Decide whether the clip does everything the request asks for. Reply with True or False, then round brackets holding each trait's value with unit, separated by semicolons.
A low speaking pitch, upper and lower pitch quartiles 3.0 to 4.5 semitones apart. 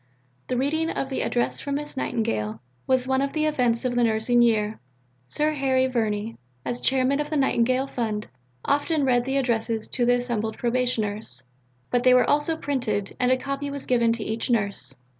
False (245 Hz; 3.4 semitones)